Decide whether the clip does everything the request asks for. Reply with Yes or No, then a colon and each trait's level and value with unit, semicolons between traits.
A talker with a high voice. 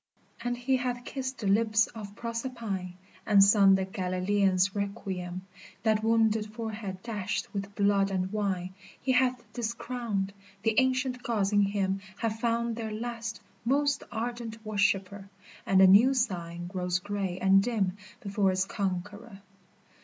Yes: high, 210 Hz